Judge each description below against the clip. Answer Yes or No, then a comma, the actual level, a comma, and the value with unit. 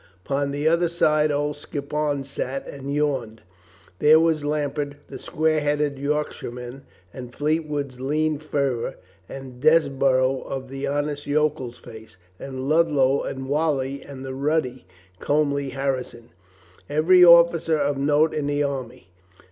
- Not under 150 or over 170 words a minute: No, average, 140 wpm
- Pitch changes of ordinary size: No, narrow, 2.2 semitones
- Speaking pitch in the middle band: Yes, medium, 145 Hz